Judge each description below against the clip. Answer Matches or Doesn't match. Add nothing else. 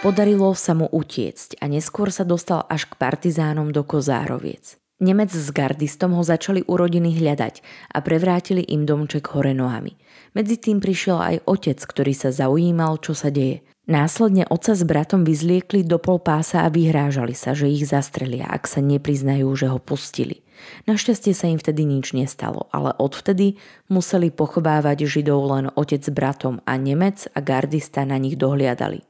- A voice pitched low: Doesn't match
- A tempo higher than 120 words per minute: Matches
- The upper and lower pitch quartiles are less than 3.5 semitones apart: Doesn't match